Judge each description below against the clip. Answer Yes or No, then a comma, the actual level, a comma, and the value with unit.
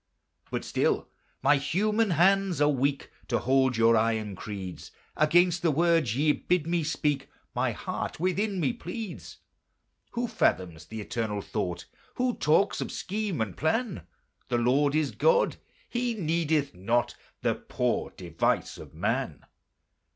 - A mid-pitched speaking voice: Yes, medium, 150 Hz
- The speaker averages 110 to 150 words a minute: Yes, average, 140 wpm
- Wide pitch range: Yes, wide, 8.2 semitones